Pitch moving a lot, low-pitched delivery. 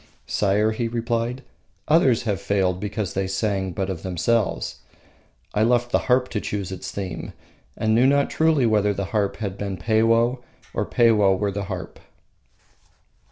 No: average, 3.3 semitones; low, 105 Hz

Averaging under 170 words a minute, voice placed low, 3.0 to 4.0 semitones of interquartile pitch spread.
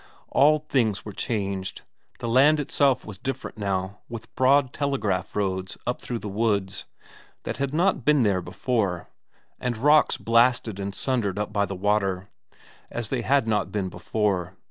No: average, 160 wpm; low, 110 Hz; average, 4.8 semitones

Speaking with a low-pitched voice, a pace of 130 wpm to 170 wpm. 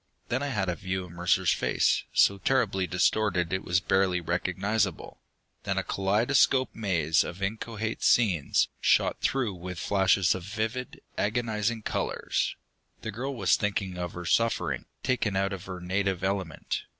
Yes: very low, 95 Hz; average, 150 wpm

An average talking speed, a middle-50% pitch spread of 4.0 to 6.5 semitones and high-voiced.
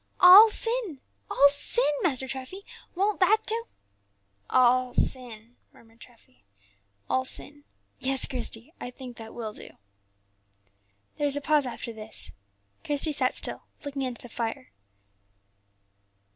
No: slow, 130 wpm; average, 4.3 semitones; very high, 265 Hz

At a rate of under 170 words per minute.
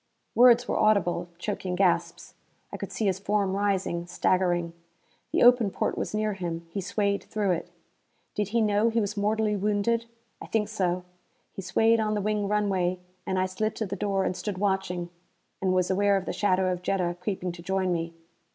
No: average, 190 wpm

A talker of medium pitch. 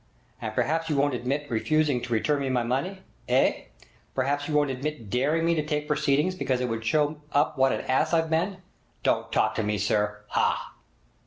Yes: medium, 145 Hz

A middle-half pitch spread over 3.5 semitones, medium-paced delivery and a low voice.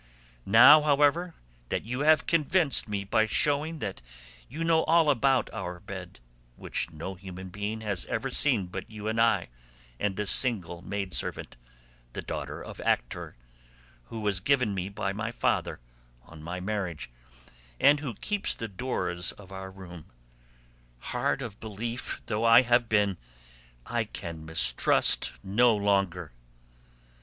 Yes: average, 5.2 semitones; average, 145 wpm; low, 105 Hz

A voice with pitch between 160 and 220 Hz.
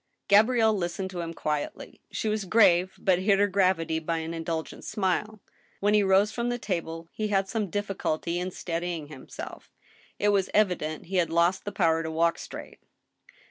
Yes: medium, 185 Hz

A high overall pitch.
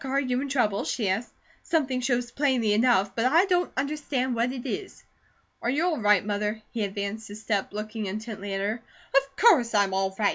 Yes: high, 235 Hz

